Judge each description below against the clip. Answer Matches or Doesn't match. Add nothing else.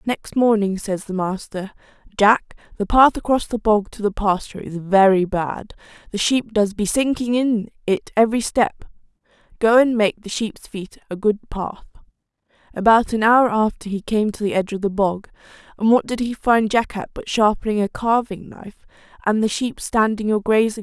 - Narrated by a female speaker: Matches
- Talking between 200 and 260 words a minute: Doesn't match